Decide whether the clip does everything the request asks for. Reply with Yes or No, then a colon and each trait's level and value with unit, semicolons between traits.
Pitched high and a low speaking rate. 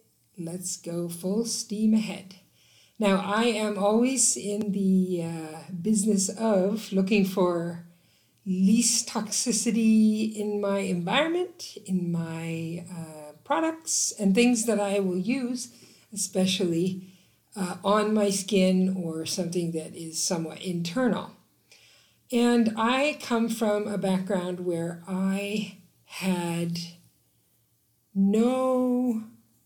Yes: high, 195 Hz; slow, 105 wpm